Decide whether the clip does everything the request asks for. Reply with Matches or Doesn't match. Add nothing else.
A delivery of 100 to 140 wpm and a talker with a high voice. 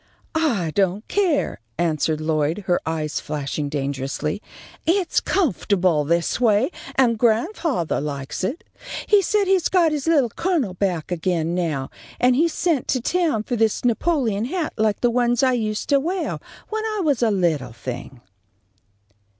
Doesn't match